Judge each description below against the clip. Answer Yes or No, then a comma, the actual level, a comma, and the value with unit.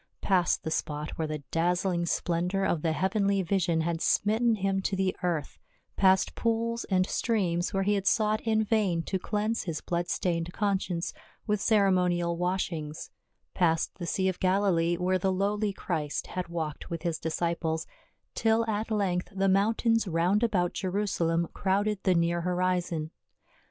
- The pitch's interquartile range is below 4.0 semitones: Yes, average, 3.0 semitones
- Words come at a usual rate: Yes, average, 160 wpm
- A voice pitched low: No, medium, 185 Hz